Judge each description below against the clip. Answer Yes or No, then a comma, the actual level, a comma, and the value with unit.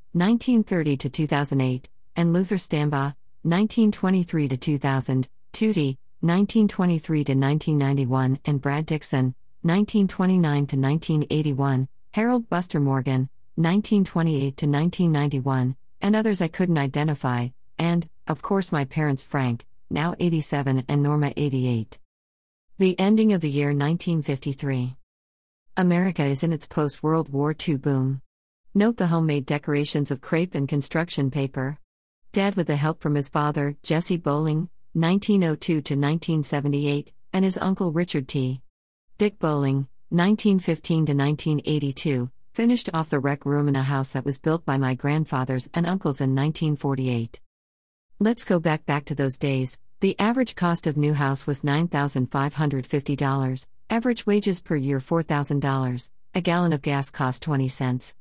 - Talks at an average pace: No, slow, 130 wpm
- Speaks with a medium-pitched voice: Yes, medium, 150 Hz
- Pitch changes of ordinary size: Yes, average, 3.9 semitones